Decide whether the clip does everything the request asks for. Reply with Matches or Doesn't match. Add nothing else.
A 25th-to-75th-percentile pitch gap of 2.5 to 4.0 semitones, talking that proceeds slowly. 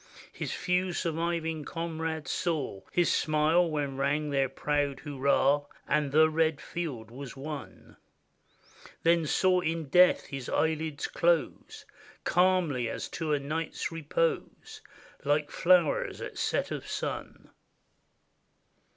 Matches